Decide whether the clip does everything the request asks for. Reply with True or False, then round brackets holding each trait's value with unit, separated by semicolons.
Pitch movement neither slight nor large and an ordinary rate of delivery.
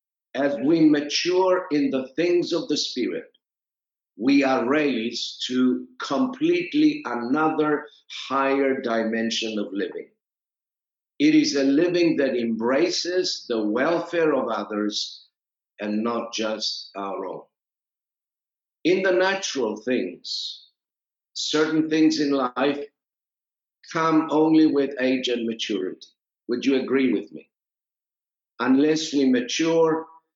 False (5.0 semitones; 110 wpm)